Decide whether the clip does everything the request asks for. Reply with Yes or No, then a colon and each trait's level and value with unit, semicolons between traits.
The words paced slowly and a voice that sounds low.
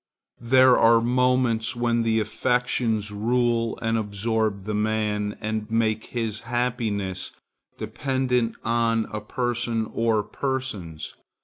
Yes: slow, 110 wpm; low, 115 Hz